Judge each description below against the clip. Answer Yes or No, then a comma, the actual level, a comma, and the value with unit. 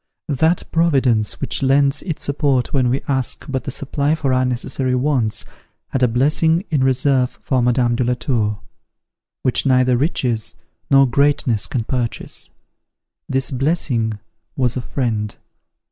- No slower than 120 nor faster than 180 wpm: Yes, average, 145 wpm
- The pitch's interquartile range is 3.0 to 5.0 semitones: No, narrow, 2.4 semitones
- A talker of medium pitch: No, low, 130 Hz